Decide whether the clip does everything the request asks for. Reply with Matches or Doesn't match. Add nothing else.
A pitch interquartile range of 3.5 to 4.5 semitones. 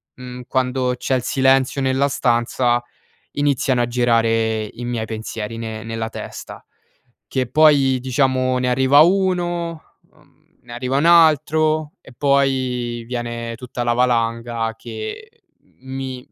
Doesn't match